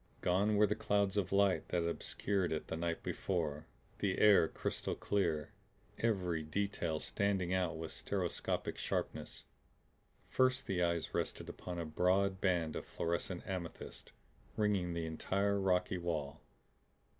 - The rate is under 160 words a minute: Yes, average, 140 wpm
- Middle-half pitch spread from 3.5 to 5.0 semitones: No, average, 3.0 semitones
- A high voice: No, very low, 90 Hz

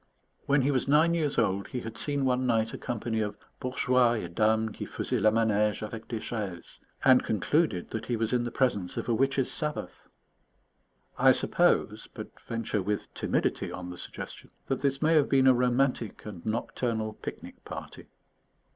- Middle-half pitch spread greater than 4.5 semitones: No, average, 3.5 semitones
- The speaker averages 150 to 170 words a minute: No, average, 180 wpm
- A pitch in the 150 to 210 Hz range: No, low, 115 Hz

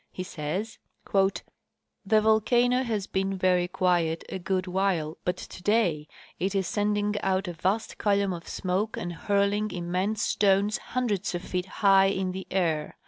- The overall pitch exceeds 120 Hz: Yes, high, 190 Hz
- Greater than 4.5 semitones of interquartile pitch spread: No, narrow, 2.4 semitones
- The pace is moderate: Yes, average, 160 wpm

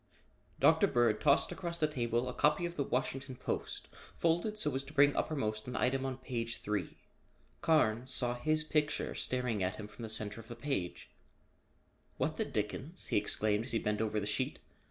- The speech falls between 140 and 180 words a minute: No, average, 190 wpm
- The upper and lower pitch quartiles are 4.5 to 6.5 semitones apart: Yes, average, 5.3 semitones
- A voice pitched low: Yes, low, 125 Hz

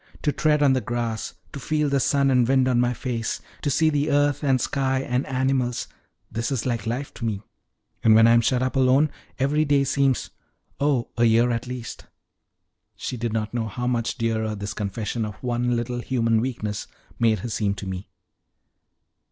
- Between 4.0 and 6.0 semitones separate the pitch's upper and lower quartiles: No, average, 2.9 semitones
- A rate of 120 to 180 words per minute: No, average, 195 wpm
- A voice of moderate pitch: No, low, 125 Hz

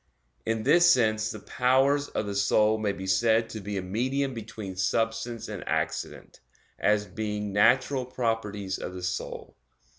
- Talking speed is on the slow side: No, average, 155 wpm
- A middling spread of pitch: Yes, average, 3.2 semitones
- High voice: No, low, 110 Hz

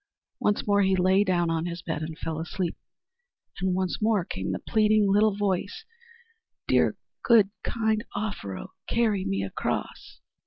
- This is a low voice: No, high, 190 Hz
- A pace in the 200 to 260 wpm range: No, average, 150 wpm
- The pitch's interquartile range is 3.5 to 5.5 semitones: Yes, average, 3.8 semitones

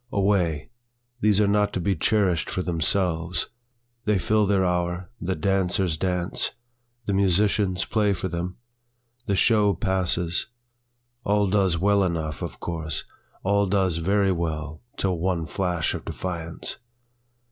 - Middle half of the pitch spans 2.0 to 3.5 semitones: Yes, average, 2.8 semitones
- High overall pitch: No, very low, 95 Hz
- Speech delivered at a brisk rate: No, slow, 135 wpm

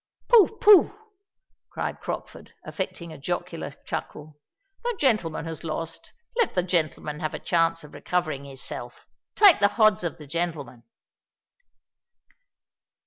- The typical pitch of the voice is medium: Yes, medium, 165 Hz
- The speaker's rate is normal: No, slow, 125 wpm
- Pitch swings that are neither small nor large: No, wide, 6.2 semitones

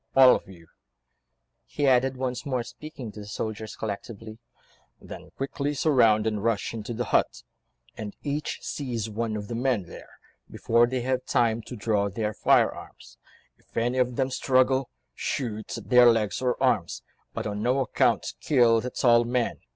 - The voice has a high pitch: No, low, 120 Hz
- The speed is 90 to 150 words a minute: No, average, 165 wpm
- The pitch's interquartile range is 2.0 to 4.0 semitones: Yes, average, 3.0 semitones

